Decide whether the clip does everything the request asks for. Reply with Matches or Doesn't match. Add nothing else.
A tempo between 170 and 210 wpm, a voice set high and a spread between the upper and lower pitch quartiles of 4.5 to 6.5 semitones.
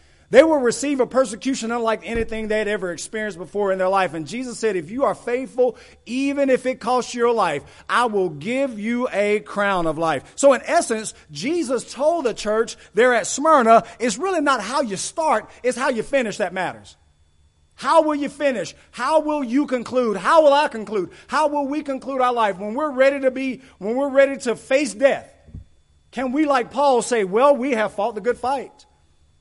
Matches